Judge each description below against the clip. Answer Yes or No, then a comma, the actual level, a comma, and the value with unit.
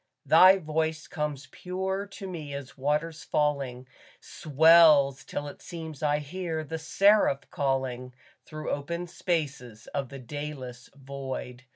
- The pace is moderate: No, slow, 130 wpm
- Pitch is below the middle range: No, medium, 150 Hz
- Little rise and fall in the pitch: No, average, 3.2 semitones